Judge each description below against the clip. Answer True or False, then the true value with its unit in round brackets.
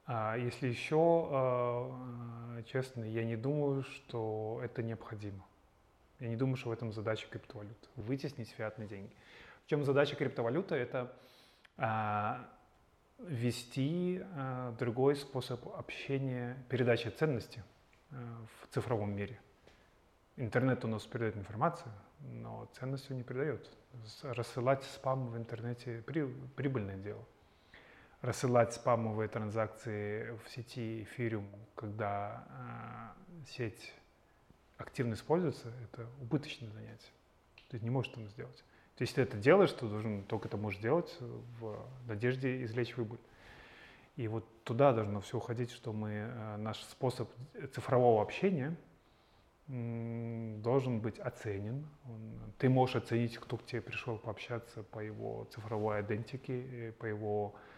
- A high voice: False (120 Hz)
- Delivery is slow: False (120 wpm)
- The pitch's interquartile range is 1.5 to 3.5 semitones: True (2.8 semitones)